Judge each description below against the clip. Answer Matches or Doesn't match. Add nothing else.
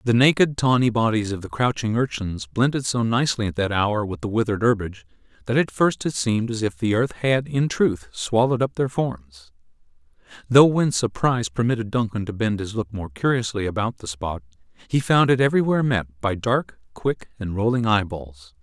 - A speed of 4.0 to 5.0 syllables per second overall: Doesn't match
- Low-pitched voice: Matches